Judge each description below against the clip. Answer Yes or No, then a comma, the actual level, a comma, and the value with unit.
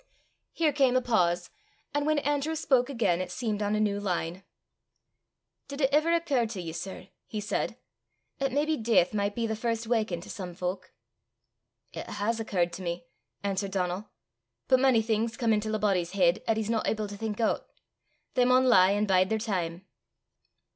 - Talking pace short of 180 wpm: No, average, 185 wpm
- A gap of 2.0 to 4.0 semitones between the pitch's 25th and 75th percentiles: No, average, 4.7 semitones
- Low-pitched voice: No, high, 215 Hz